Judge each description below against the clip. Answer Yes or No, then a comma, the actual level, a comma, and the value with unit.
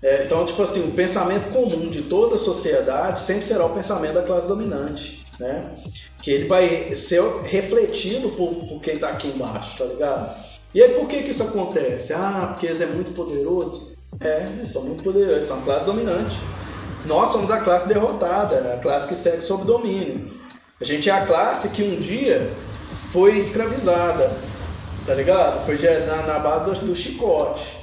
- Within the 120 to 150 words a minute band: No, fast, 185 wpm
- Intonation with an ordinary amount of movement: No, wide, 5.8 semitones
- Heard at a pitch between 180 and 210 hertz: Yes, medium, 185 Hz